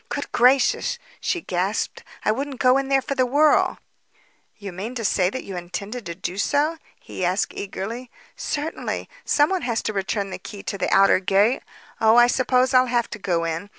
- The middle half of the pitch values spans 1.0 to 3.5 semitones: No, average, 4.9 semitones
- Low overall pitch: No, high, 225 Hz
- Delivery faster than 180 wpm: Yes, average, 195 wpm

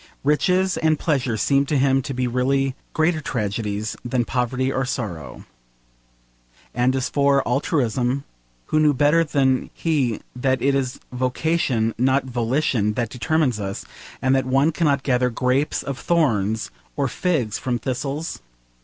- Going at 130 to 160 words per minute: Yes, average, 145 wpm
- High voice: No, low, 130 Hz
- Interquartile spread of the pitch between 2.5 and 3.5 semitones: Yes, average, 2.9 semitones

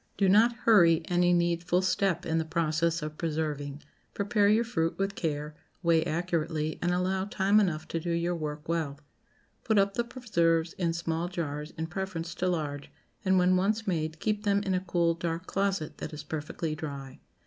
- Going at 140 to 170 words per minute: No, average, 180 wpm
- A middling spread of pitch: Yes, average, 3.2 semitones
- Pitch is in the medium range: Yes, medium, 170 Hz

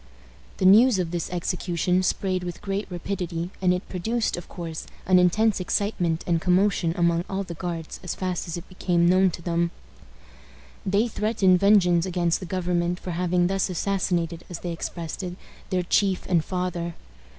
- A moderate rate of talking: Yes, average, 170 wpm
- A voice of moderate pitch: Yes, medium, 180 Hz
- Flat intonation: Yes, narrow, 1.7 semitones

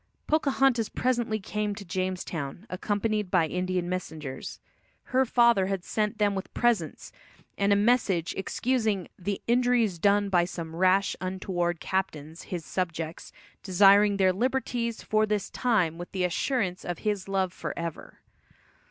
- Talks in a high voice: Yes, high, 195 Hz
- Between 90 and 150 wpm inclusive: Yes, slow, 135 wpm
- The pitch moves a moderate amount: Yes, average, 3.4 semitones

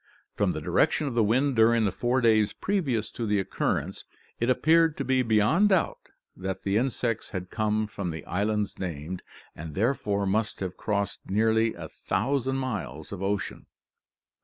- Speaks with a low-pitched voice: Yes, low, 110 Hz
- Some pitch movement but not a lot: Yes, average, 4.6 semitones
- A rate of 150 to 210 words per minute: Yes, average, 165 wpm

